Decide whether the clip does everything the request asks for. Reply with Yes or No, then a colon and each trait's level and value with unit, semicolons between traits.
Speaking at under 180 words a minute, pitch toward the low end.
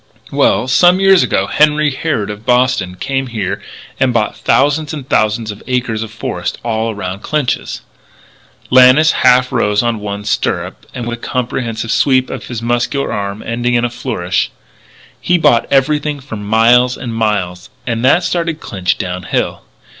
Yes: average, 170 wpm; low, 120 Hz